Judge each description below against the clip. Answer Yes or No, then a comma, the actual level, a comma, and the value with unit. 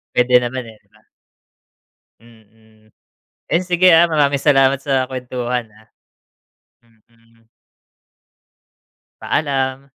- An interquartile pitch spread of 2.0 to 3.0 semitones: No, average, 3.4 semitones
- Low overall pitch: Yes, low, 125 Hz